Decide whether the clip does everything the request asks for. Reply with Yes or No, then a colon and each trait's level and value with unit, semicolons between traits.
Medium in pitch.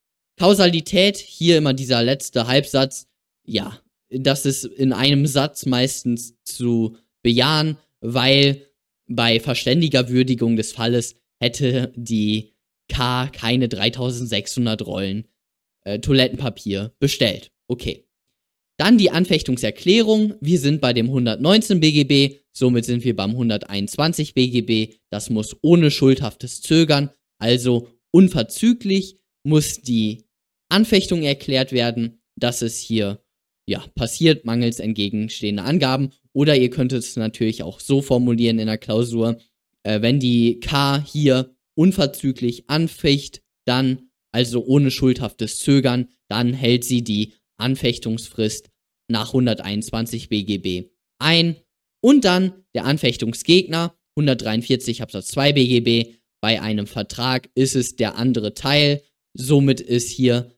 No: low, 125 Hz